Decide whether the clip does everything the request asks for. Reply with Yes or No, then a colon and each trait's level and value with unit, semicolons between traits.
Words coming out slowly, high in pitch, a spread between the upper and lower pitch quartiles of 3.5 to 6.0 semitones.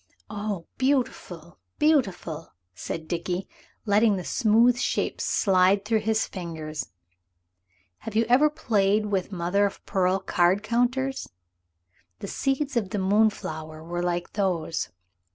Yes: slow, 120 wpm; high, 200 Hz; average, 4.3 semitones